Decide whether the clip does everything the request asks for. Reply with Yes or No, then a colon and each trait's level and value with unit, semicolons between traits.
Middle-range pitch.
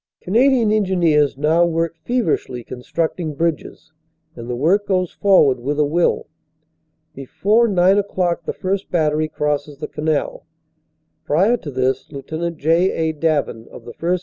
Yes: medium, 160 Hz